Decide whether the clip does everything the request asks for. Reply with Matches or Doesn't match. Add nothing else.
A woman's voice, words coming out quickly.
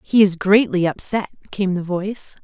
Doesn't match